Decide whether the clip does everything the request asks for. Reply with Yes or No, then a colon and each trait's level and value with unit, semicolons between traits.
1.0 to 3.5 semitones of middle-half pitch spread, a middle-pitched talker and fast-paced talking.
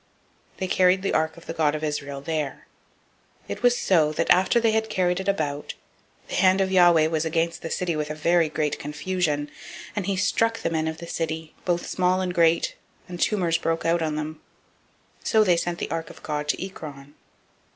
Yes: average, 3.1 semitones; medium, 165 Hz; fast, 210 wpm